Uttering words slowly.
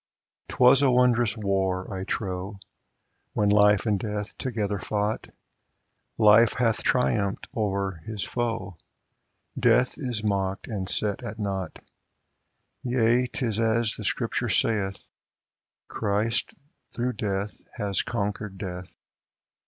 Yes: slow, 115 wpm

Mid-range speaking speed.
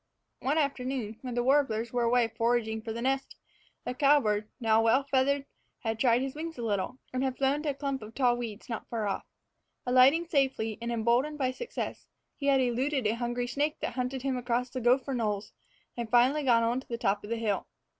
No: fast, 210 wpm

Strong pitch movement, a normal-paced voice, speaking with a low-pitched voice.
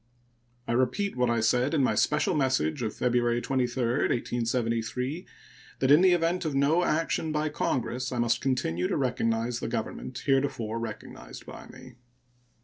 No: average, 3.2 semitones; average, 155 wpm; low, 125 Hz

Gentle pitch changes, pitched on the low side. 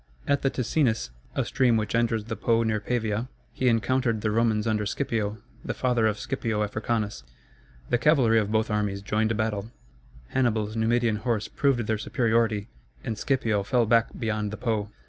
Yes: narrow, 1.9 semitones; low, 110 Hz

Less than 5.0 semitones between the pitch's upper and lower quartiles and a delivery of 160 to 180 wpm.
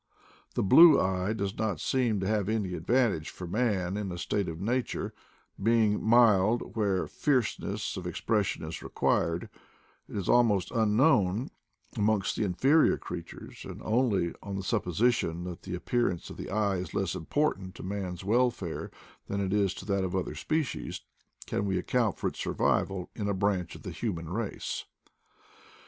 Yes: average, 3.5 semitones; average, 170 wpm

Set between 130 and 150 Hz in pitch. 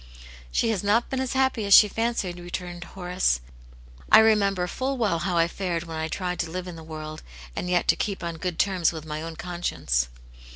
No: medium, 180 Hz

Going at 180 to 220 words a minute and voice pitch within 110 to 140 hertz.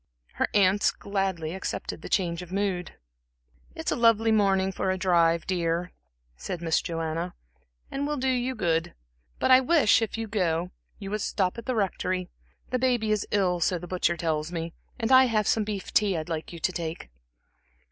No: average, 190 wpm; high, 190 Hz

